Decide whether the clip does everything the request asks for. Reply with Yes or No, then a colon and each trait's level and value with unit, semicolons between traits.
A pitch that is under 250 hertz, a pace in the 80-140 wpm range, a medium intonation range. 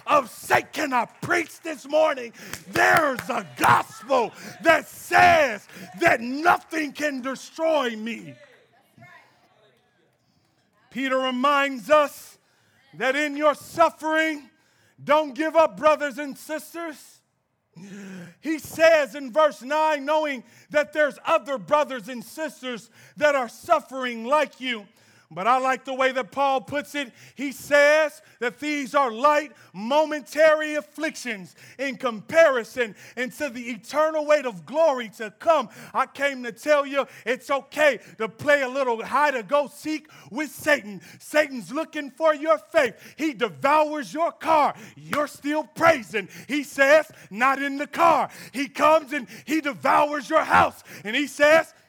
No: very high, 285 Hz; slow, 135 wpm; average, 3.5 semitones